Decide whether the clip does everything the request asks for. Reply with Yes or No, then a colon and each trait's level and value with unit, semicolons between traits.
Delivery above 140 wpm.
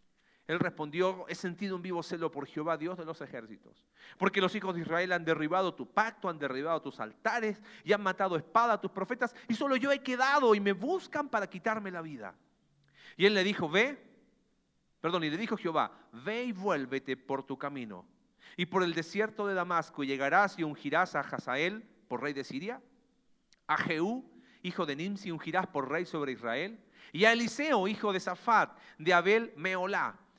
Yes: fast, 190 wpm